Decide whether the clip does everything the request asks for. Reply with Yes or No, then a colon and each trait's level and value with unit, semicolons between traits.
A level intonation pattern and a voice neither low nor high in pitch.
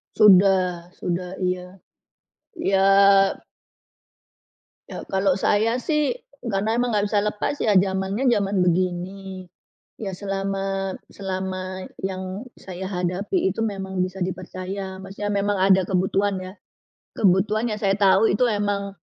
No: narrow, 1.7 semitones; high, 195 Hz